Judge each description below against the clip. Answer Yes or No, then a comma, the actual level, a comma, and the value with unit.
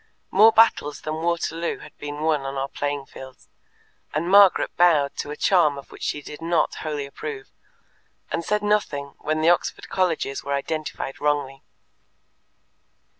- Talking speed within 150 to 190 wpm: Yes, average, 155 wpm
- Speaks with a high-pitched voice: No, medium, 155 Hz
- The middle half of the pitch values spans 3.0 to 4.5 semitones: Yes, average, 3.5 semitones